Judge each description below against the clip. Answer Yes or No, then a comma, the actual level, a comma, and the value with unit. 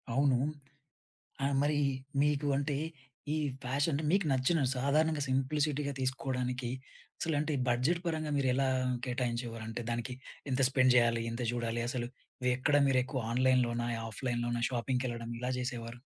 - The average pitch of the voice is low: Yes, low, 130 Hz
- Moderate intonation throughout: Yes, average, 3.0 semitones